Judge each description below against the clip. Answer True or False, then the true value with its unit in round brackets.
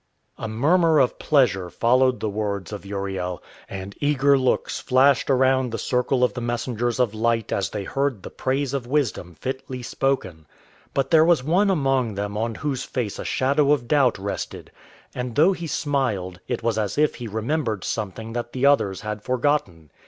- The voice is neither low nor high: False (125 Hz)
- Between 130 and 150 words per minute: False (180 wpm)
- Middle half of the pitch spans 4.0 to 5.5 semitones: True (4.6 semitones)